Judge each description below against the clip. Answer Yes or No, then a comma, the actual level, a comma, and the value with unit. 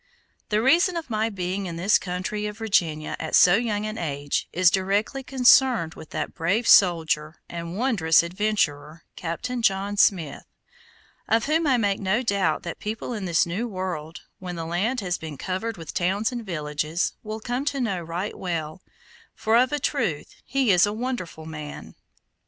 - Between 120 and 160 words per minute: No, average, 175 wpm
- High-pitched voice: Yes, high, 195 Hz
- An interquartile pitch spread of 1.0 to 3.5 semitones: No, average, 5.1 semitones